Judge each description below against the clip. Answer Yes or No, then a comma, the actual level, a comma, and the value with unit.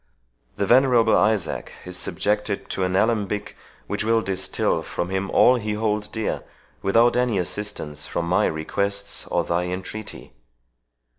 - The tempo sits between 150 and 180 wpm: No, average, 140 wpm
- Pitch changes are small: No, average, 3.0 semitones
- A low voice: Yes, low, 105 Hz